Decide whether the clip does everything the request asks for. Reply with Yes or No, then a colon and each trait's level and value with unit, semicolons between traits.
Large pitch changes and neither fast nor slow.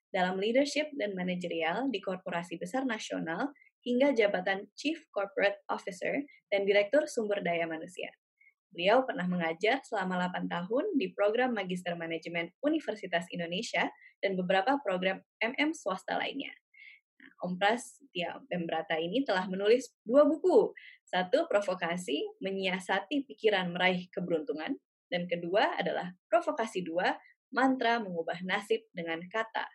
No: wide, 7.3 semitones; slow, 125 wpm